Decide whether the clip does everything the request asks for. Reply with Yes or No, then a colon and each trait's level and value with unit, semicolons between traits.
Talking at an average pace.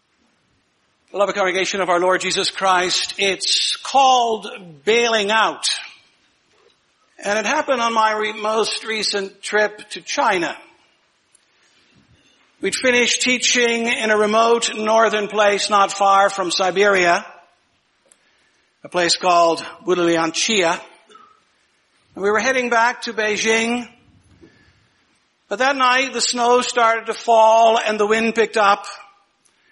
No: slow, 120 wpm